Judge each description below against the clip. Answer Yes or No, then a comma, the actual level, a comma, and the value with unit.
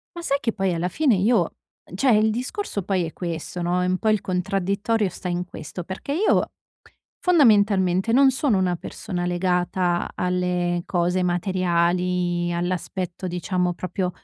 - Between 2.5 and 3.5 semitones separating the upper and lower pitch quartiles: Yes, average, 2.9 semitones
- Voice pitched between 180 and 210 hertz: Yes, medium, 185 Hz